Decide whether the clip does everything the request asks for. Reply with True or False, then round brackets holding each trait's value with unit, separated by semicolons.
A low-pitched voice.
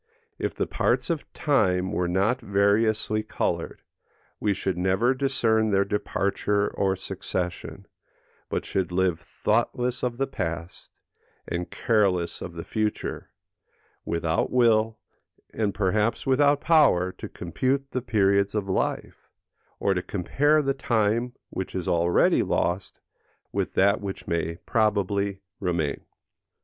True (100 Hz)